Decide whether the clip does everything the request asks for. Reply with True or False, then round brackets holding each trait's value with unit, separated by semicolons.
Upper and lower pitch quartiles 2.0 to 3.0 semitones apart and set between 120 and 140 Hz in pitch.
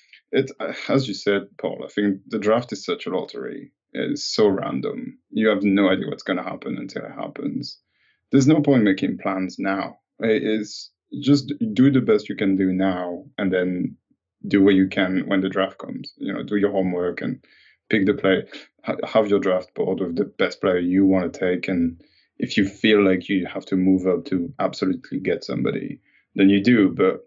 False (2.5 semitones; 100 Hz)